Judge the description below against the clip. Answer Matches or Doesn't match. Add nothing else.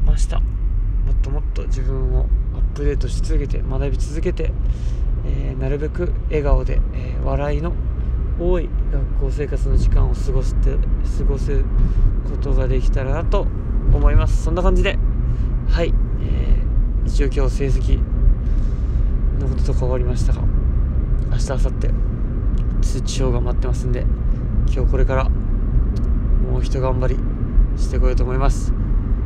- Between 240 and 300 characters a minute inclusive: Matches